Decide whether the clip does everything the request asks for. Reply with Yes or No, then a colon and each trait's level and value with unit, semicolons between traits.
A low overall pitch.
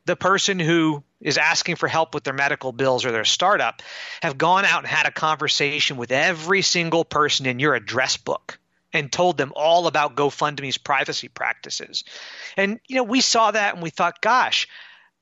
No: medium, 160 Hz